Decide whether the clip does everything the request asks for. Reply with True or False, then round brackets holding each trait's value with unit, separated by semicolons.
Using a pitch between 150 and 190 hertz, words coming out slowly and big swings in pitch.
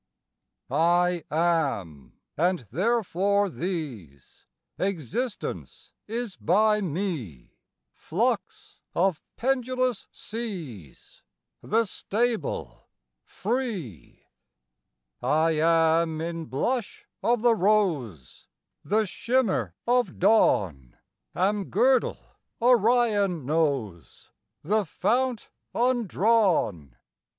True (185 Hz; 75 wpm; 6.7 semitones)